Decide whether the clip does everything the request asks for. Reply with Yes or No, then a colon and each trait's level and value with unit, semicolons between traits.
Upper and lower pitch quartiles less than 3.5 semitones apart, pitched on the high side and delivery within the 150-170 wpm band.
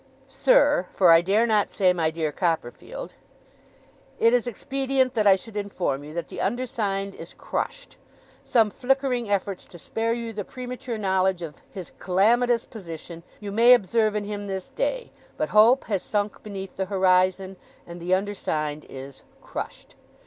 No: average, 4.3 semitones; high, 205 Hz; average, 160 wpm